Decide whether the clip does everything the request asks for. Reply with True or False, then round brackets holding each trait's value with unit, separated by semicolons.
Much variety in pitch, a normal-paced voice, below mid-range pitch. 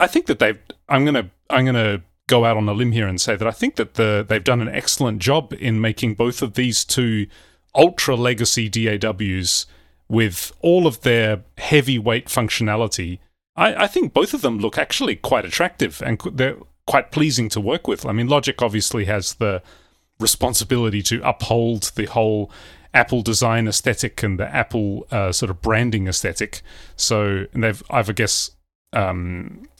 False (3.6 semitones; 180 wpm; 110 Hz)